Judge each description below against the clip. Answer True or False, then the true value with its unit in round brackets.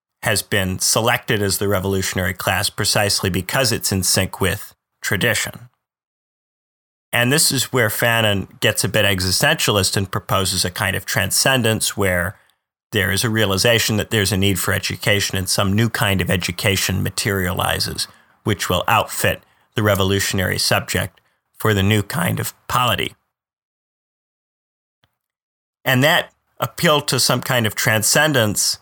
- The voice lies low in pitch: True (105 Hz)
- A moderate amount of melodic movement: True (3.4 semitones)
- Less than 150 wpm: True (140 wpm)